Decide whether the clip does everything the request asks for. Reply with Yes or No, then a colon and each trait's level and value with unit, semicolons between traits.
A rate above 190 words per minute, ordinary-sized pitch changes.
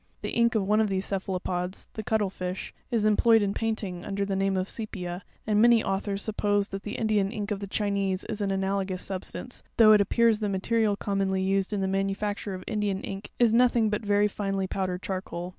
No: fast, 205 wpm; narrow, 1.9 semitones